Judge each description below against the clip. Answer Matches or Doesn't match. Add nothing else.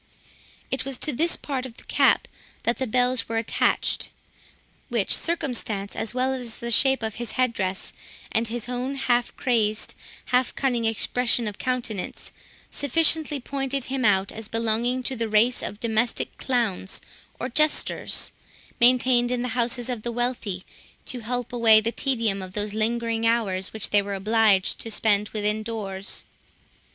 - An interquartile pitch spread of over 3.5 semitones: Doesn't match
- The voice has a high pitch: Matches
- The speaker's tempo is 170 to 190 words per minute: Doesn't match